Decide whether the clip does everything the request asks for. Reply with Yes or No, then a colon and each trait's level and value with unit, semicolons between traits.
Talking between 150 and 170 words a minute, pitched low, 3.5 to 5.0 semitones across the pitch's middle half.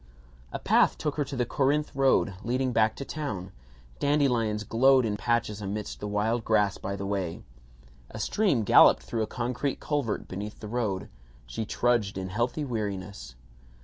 Yes: average, 165 wpm; low, 110 Hz; average, 4.1 semitones